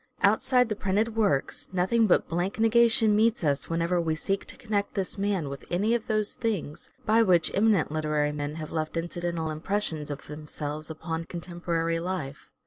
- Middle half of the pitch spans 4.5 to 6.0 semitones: Yes, average, 5.1 semitones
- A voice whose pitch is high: No, medium, 175 Hz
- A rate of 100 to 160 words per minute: No, average, 170 wpm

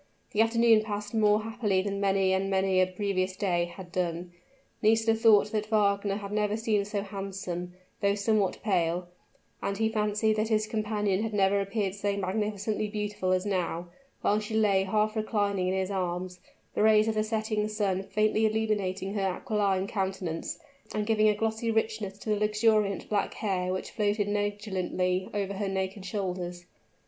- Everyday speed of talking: Yes, average, 170 wpm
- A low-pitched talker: No, high, 205 Hz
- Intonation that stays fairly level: Yes, narrow, 2.0 semitones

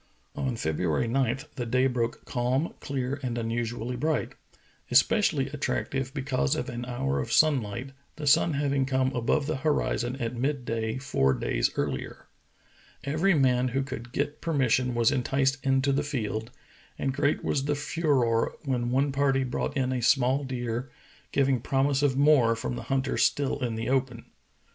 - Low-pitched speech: Yes, low, 130 Hz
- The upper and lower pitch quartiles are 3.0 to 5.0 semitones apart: No, narrow, 2.6 semitones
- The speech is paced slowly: No, average, 170 wpm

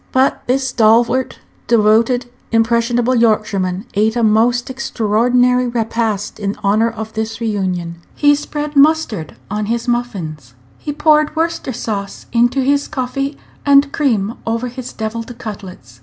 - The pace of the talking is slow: Yes, slow, 130 wpm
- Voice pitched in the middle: No, high, 235 Hz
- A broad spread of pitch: No, average, 3.3 semitones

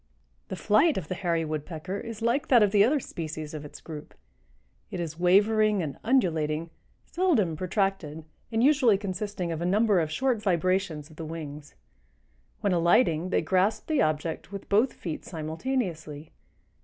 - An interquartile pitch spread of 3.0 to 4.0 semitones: No, average, 5.2 semitones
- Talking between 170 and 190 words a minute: No, average, 160 wpm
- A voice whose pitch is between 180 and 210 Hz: Yes, medium, 185 Hz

